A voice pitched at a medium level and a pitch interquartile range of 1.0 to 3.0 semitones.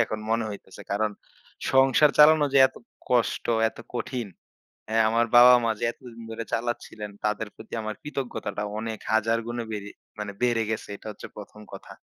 No: low, 115 Hz; narrow, 2.4 semitones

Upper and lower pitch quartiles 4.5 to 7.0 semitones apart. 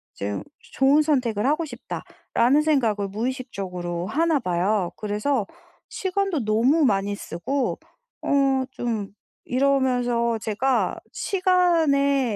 Yes: average, 5.3 semitones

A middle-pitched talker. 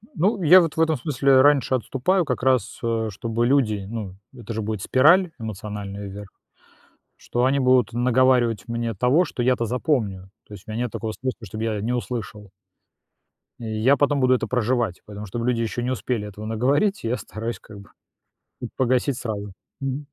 No: low, 120 Hz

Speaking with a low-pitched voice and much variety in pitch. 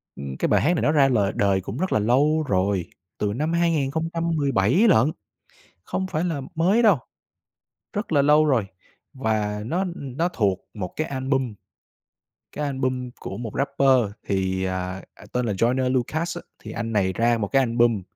Yes: low, 130 Hz; wide, 6.8 semitones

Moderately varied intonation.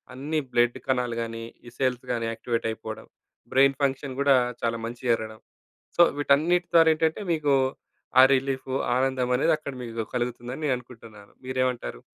Yes: average, 3.0 semitones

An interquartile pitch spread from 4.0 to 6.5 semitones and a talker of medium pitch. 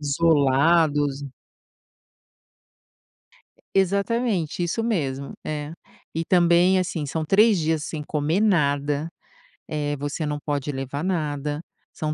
No: average, 3.2 semitones; medium, 155 Hz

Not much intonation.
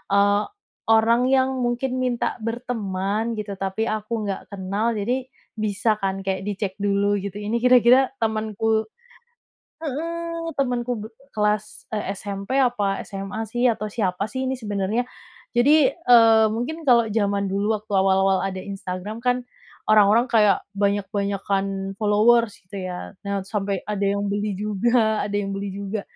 No: average, 3.1 semitones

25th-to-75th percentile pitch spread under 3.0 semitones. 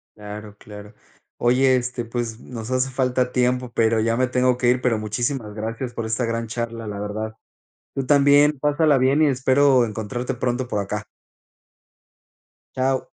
Yes: narrow, 2.6 semitones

